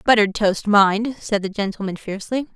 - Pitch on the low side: No, high, 205 Hz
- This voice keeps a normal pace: Yes, average, 165 wpm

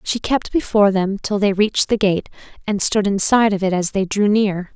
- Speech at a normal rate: No, fast, 225 wpm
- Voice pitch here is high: Yes, high, 200 Hz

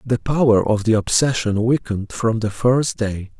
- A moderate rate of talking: Yes, average, 175 wpm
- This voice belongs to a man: Yes, male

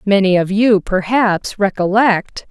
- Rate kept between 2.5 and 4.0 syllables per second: Yes, 3.8 syllables/s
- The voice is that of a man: No, female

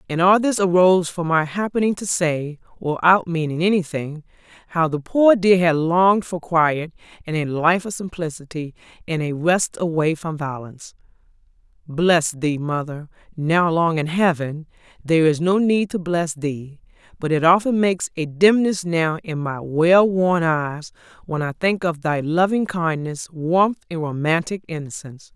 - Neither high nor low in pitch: Yes, medium, 165 Hz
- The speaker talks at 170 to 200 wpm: No, average, 160 wpm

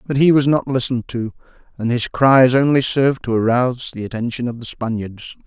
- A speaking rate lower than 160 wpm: No, average, 200 wpm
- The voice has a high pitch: No, low, 125 Hz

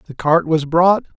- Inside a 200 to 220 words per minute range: Yes, fast, 205 wpm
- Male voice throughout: Yes, male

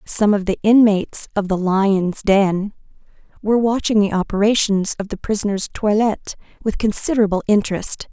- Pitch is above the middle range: Yes, high, 205 Hz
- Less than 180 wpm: Yes, average, 140 wpm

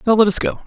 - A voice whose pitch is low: No, high, 215 Hz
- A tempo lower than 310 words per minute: No, fast, 360 wpm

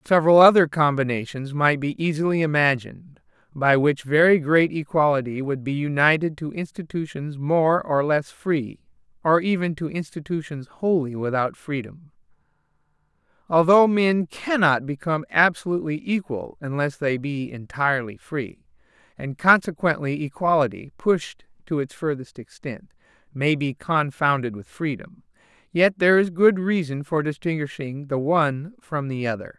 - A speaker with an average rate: No, slow, 130 wpm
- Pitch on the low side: No, medium, 155 Hz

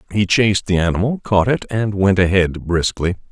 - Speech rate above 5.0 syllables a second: Yes, 5.2 syllables/s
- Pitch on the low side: Yes, low, 100 Hz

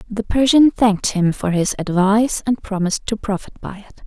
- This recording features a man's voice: No, female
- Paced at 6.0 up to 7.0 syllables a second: No, 5.4 syllables/s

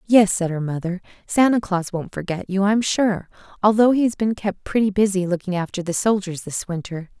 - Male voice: No, female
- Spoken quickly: Yes, fast, 210 wpm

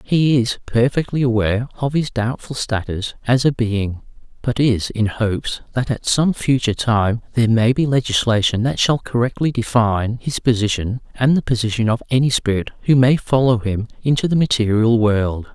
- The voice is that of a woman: No, male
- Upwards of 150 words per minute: Yes, average, 170 wpm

